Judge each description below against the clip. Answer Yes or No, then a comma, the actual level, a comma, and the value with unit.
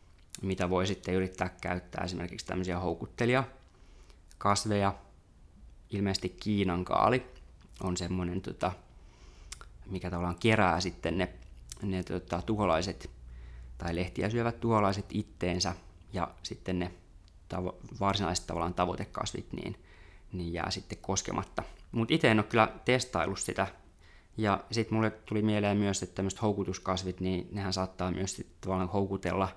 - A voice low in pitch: Yes, very low, 95 Hz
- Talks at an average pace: Yes, average, 125 wpm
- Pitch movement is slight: Yes, narrow, 2.3 semitones